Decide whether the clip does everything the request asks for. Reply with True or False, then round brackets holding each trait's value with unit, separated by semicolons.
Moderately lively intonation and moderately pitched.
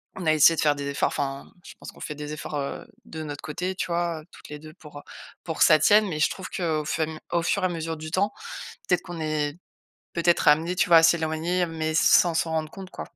False (2.1 semitones; 160 Hz)